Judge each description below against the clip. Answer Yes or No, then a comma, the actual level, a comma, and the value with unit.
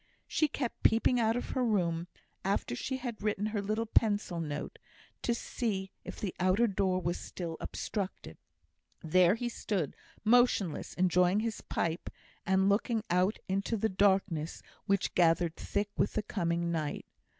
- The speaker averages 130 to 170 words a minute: Yes, average, 150 wpm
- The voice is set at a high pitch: Yes, high, 195 Hz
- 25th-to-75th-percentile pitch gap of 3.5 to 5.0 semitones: Yes, average, 3.9 semitones